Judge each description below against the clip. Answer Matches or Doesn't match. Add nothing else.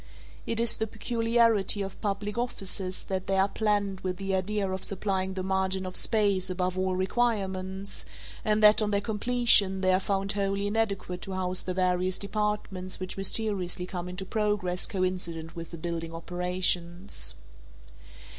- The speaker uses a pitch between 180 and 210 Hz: Matches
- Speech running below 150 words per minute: Doesn't match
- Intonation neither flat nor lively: Doesn't match